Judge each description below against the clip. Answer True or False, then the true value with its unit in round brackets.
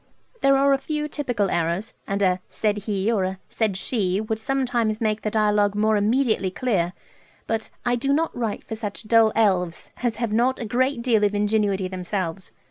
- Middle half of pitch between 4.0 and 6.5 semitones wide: False (3.3 semitones)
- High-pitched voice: True (215 Hz)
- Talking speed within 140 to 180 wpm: False (190 wpm)